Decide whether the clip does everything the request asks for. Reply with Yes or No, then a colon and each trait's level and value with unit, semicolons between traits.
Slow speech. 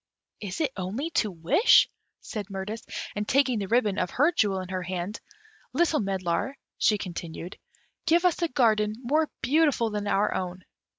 No: average, 165 wpm